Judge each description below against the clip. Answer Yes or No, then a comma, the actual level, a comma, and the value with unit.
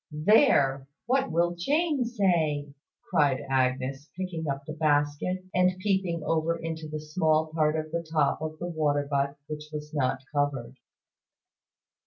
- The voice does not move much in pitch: No, average, 3.2 semitones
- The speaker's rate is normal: Yes, average, 145 wpm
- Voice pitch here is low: No, medium, 155 Hz